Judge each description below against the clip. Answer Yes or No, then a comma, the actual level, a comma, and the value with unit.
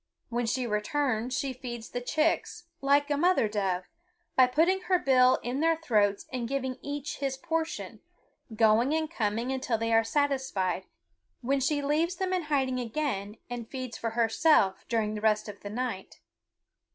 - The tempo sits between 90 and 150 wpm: No, average, 165 wpm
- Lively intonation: No, average, 4.5 semitones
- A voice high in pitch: Yes, very high, 255 Hz